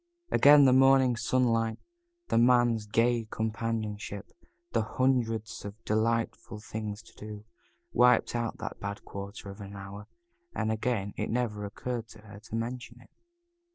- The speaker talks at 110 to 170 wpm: Yes, average, 145 wpm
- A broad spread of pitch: No, narrow, 2.5 semitones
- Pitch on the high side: No, low, 115 Hz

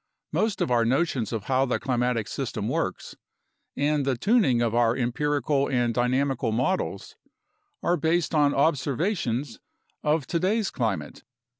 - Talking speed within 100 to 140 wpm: Yes, slow, 135 wpm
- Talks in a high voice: No, low, 135 Hz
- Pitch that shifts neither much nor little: Yes, average, 4.1 semitones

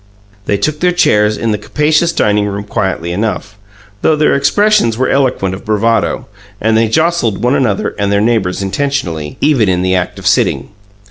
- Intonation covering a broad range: Yes, wide, 5.8 semitones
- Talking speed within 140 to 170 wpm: No, average, 180 wpm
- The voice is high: No, low, 110 Hz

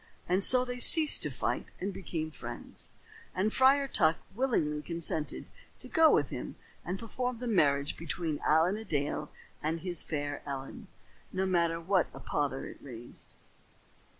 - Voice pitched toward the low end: No, medium, 170 Hz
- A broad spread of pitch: Yes, wide, 6.4 semitones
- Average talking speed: Yes, average, 155 wpm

